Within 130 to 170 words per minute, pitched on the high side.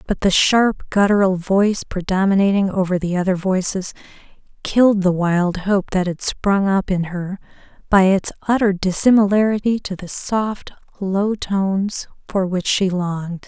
Yes: average, 145 wpm; high, 195 Hz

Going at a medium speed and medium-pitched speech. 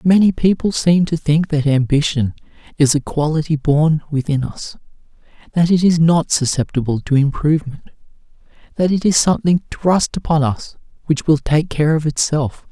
Yes: average, 155 wpm; medium, 155 Hz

